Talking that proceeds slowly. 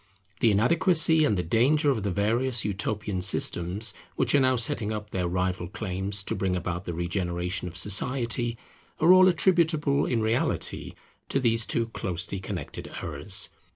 No: average, 155 wpm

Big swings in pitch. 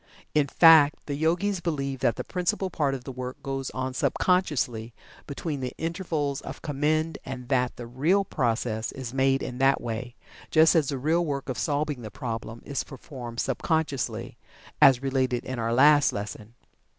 No: average, 3.8 semitones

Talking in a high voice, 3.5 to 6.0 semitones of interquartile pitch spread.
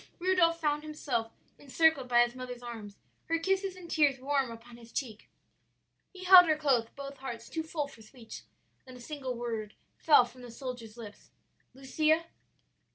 Yes: very high, 265 Hz; average, 4.7 semitones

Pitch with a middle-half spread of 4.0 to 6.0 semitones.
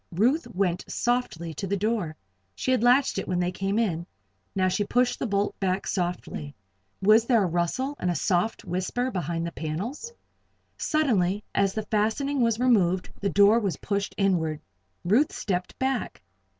Yes: average, 4.9 semitones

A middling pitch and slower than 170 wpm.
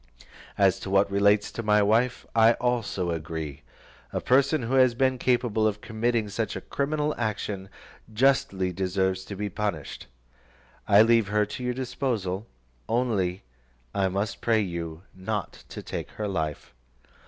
No: low, 105 Hz; average, 150 wpm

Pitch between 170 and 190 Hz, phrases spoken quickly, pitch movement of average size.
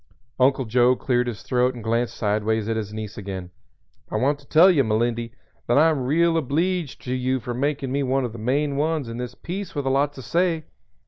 No: low, 130 Hz; fast, 220 wpm; average, 3.8 semitones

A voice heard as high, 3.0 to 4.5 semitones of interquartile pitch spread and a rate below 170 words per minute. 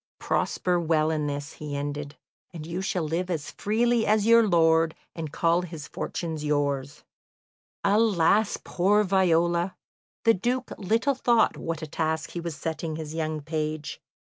No: medium, 165 Hz; average, 3.8 semitones; average, 150 wpm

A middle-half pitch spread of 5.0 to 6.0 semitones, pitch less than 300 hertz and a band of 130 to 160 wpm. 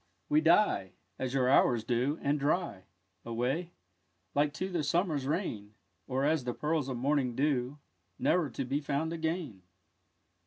No: average, 4.3 semitones; medium, 140 Hz; average, 150 wpm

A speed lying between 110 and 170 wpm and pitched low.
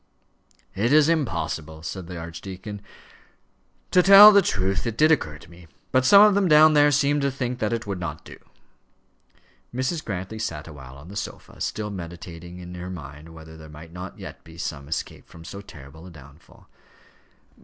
No: average, 185 wpm; very low, 90 Hz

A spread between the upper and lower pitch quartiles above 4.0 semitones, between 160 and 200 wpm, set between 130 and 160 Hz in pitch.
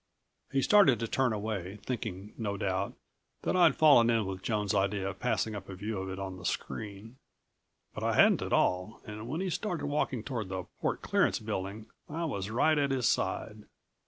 No: average, 5.1 semitones; average, 195 wpm; low, 110 Hz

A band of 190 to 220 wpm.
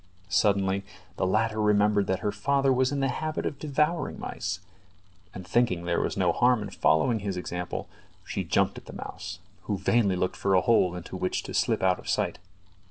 Yes: average, 195 wpm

